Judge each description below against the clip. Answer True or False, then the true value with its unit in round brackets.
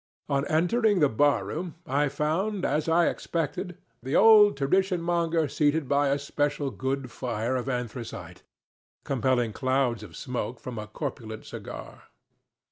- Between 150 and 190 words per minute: False (140 wpm)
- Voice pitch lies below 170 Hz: True (140 Hz)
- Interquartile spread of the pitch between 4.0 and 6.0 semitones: True (4.5 semitones)